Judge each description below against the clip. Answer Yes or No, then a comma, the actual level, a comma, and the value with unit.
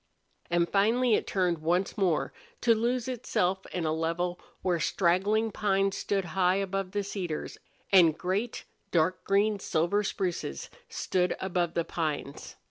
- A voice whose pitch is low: No, medium, 185 Hz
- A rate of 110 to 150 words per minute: Yes, average, 140 wpm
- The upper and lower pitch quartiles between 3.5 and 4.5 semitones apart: No, average, 2.8 semitones